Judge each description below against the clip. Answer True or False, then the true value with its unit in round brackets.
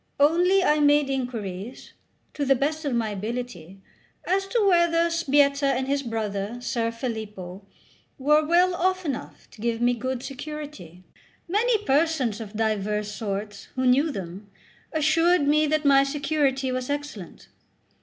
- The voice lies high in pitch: True (270 Hz)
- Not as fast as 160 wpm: True (145 wpm)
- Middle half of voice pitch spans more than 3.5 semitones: True (5.6 semitones)